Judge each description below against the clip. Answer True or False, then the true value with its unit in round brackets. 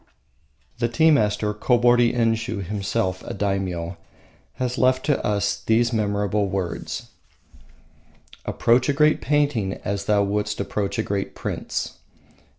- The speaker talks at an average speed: False (125 wpm)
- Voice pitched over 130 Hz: False (105 Hz)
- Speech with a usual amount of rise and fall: True (3.4 semitones)